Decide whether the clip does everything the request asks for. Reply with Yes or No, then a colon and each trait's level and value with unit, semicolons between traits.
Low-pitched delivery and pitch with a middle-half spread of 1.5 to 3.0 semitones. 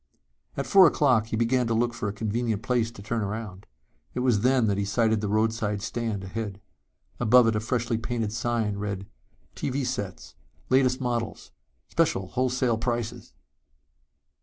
Yes: low, 115 Hz; average, 2.7 semitones